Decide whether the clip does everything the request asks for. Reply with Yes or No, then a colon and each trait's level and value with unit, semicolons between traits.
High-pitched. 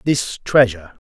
No: low, 115 Hz